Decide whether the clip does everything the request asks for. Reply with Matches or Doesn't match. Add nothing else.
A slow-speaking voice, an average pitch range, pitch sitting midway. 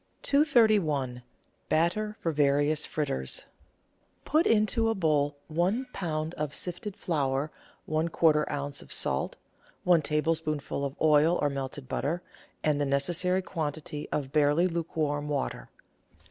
Matches